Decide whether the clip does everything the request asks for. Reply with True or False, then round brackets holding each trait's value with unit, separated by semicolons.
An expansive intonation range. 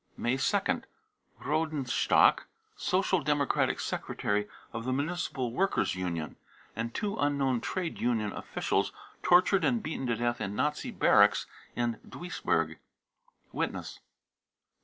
True (6.7 semitones)